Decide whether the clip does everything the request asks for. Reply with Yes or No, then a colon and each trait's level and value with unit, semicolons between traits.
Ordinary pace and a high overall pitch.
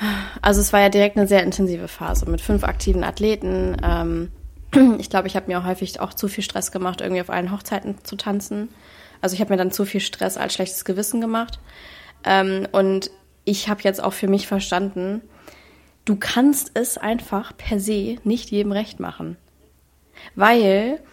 Yes: average, 175 wpm; high, 200 Hz